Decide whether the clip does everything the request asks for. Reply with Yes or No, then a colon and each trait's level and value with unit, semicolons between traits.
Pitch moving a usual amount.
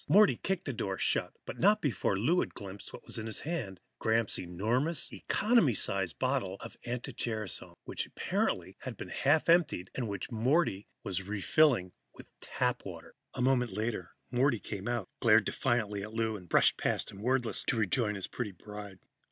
Yes: average, 4.8 semitones